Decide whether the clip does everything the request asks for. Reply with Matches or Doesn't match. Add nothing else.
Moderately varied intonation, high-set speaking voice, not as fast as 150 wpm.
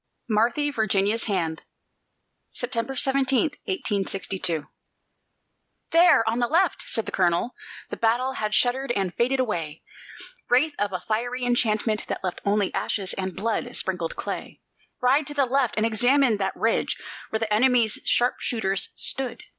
Matches